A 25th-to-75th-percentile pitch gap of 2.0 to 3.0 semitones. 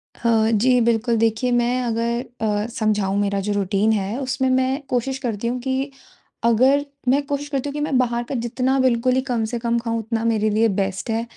Yes: average, 2.7 semitones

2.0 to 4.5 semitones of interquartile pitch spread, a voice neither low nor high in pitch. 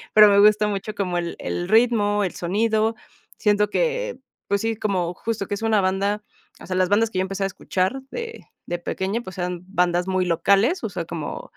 No: average, 2.9 semitones; high, 205 Hz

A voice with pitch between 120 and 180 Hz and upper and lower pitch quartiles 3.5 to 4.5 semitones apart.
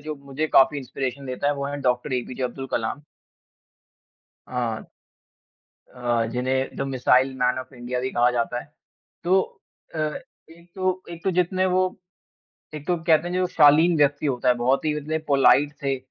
Yes: medium, 140 Hz; average, 3.8 semitones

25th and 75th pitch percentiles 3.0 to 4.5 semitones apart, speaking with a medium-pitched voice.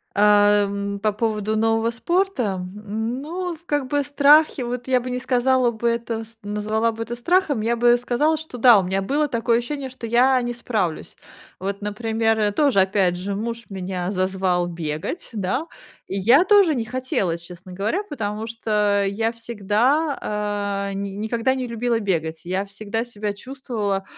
No: average, 3.9 semitones; high, 225 Hz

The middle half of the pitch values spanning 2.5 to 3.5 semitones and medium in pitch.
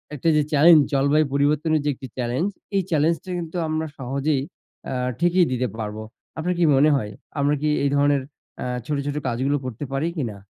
Yes: average, 2.8 semitones; medium, 145 Hz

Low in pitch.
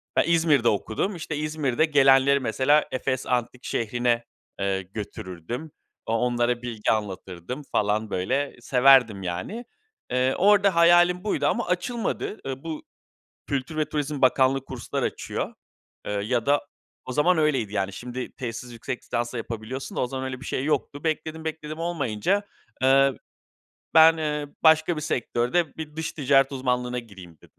Yes: low, 130 Hz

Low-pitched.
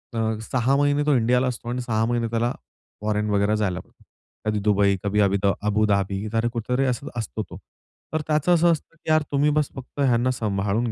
Yes: low, 115 Hz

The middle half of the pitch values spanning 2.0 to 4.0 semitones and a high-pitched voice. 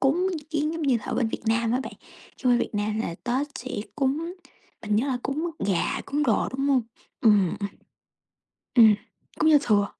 No: average, 5.0 semitones; very high, 255 Hz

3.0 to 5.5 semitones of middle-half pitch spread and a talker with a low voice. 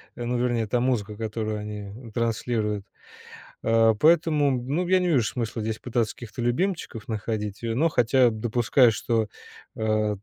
No: narrow, 2.5 semitones; low, 115 Hz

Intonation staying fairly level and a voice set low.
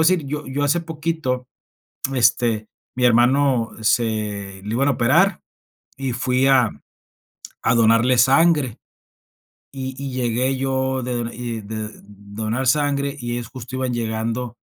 No: average, 3.0 semitones; low, 125 Hz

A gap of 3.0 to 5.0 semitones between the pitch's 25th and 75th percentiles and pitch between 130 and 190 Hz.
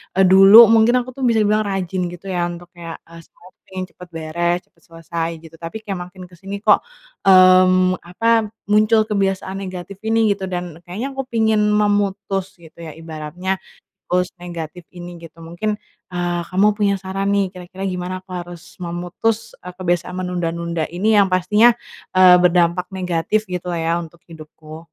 No: narrow, 2.6 semitones; medium, 185 Hz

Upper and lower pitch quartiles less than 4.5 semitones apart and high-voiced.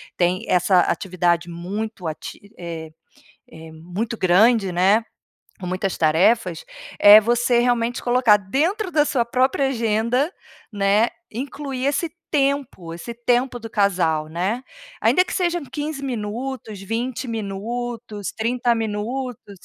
No: average, 5.0 semitones; high, 225 Hz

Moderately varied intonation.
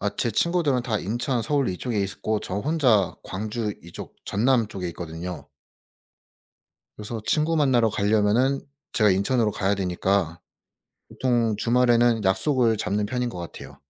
Yes: average, 3.9 semitones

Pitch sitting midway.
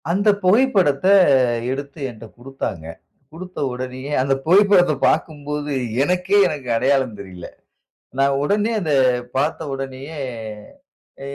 Yes: medium, 145 Hz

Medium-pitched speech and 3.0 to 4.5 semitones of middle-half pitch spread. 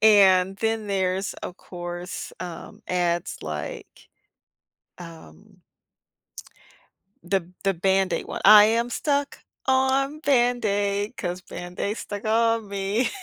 No: high, 200 Hz; average, 3.8 semitones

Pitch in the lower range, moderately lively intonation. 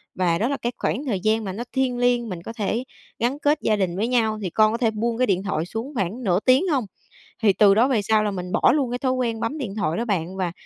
No: high, 220 Hz; average, 4.1 semitones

